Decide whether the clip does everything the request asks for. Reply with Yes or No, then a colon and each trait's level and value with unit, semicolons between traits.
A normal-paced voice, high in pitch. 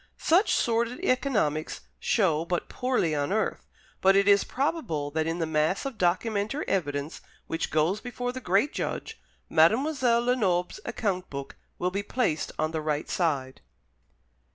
Yes: average, 150 wpm; high, 195 Hz